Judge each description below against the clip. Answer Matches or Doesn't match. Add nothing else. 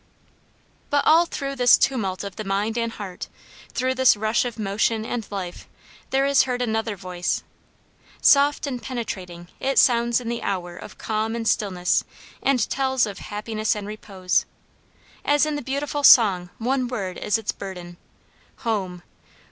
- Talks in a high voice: Matches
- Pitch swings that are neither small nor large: Matches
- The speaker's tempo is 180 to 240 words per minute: Doesn't match